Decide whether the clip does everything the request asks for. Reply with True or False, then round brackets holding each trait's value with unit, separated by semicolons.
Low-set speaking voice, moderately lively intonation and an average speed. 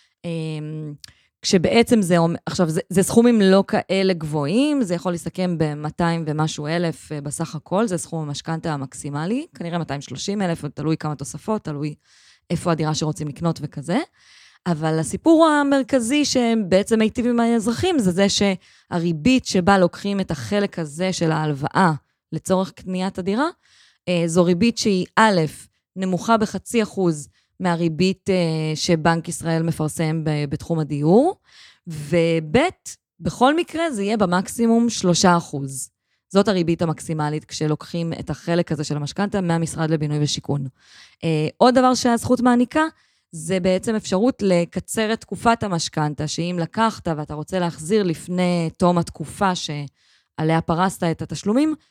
False (175 Hz; 4.4 semitones; 130 wpm)